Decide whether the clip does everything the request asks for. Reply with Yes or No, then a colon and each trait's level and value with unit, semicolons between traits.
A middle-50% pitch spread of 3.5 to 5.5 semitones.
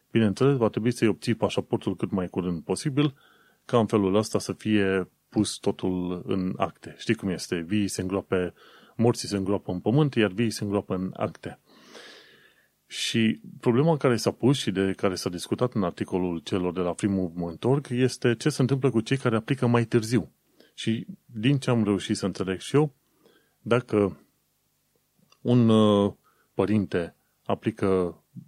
Yes: average, 4.1 semitones